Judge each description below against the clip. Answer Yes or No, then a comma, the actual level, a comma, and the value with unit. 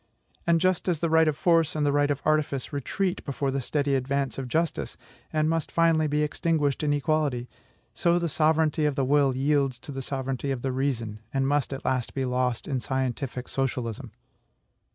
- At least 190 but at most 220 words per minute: Yes, average, 195 wpm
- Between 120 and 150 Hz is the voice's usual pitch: Yes, medium, 140 Hz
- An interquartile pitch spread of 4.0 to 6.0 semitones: No, average, 2.7 semitones